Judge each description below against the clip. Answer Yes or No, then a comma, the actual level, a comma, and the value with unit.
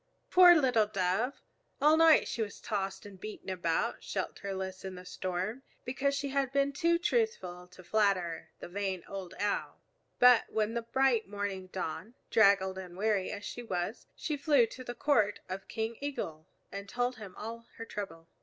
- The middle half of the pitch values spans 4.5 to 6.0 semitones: Yes, average, 4.9 semitones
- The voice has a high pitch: Yes, high, 210 Hz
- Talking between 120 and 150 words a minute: No, average, 175 wpm